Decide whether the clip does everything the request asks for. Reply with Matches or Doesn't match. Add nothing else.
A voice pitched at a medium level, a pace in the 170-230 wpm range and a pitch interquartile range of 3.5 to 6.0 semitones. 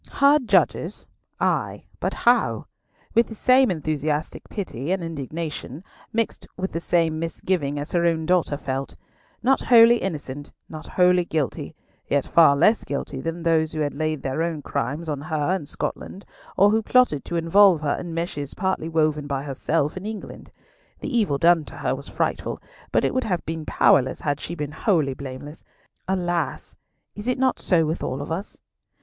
Matches